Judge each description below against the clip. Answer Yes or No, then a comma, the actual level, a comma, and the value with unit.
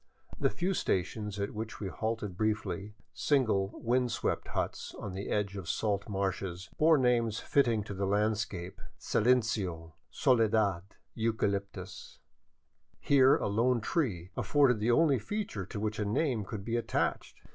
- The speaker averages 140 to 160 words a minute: Yes, average, 150 wpm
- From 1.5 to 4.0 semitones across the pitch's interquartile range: Yes, average, 3.4 semitones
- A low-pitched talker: Yes, low, 105 Hz